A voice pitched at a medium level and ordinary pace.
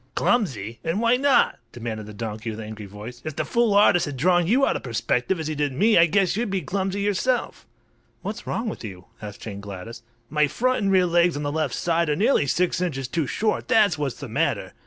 No: medium, 160 Hz; fast, 225 wpm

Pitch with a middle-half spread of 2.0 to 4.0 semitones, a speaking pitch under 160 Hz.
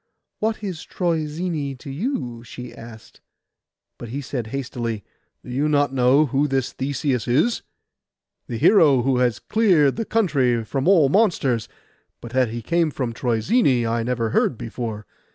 No: average, 4.7 semitones; low, 135 Hz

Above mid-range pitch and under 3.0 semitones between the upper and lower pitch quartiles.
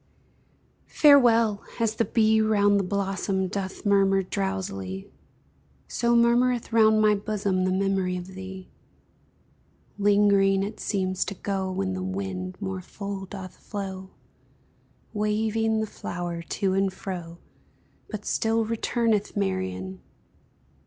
Yes: high, 195 Hz; narrow, 2.4 semitones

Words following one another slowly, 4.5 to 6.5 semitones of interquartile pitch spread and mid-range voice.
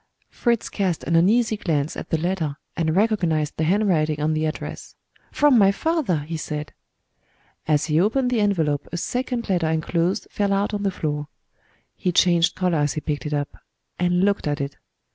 No: average, 180 wpm; average, 4.8 semitones; medium, 170 Hz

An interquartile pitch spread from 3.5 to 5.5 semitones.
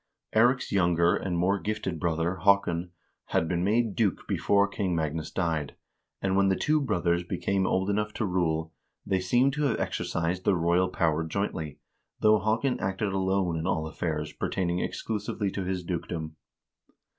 No: average, 3.1 semitones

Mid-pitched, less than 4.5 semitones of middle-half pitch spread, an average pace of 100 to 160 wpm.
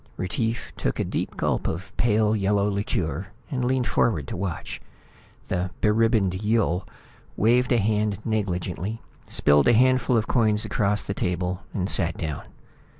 No: low, 105 Hz; average, 3.7 semitones; average, 150 wpm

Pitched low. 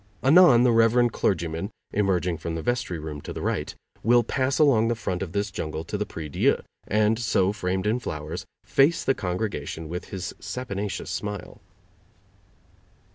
Yes: low, 100 Hz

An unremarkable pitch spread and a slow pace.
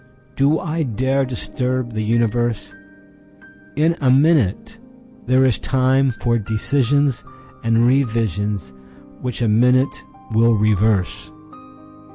Yes: average, 4.0 semitones; slow, 90 wpm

